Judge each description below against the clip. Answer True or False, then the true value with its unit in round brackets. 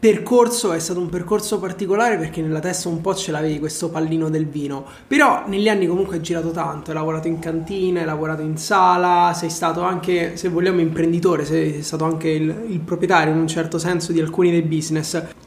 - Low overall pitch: False (170 Hz)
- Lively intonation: False (2.4 semitones)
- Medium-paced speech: False (200 wpm)